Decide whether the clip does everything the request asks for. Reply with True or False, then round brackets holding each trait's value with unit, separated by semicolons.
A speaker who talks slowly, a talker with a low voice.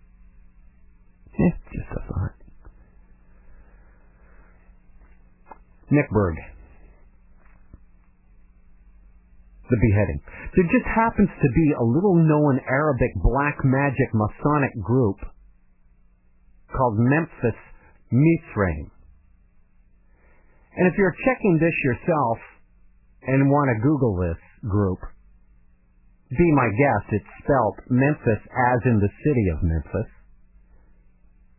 True (85 wpm; 105 Hz)